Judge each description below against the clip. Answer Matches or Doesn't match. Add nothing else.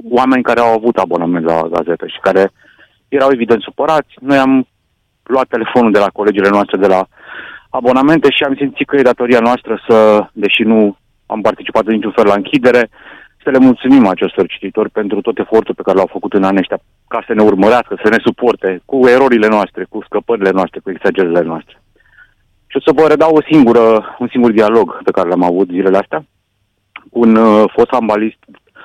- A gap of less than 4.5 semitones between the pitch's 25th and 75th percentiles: Matches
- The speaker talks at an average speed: Doesn't match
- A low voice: Matches